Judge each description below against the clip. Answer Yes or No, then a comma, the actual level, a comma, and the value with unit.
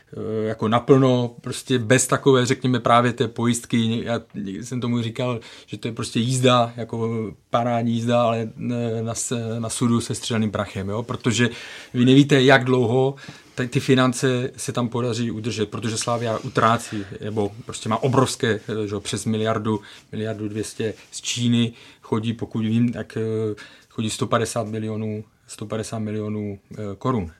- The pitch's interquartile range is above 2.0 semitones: Yes, narrow, 2.5 semitones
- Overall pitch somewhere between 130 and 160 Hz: No, low, 115 Hz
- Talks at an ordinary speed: Yes, average, 140 wpm